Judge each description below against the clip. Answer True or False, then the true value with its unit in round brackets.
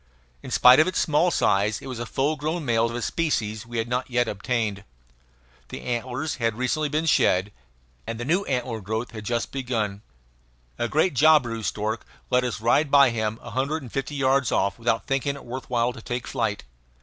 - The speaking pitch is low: True (125 Hz)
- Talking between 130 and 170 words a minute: False (200 wpm)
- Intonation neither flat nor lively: True (3.6 semitones)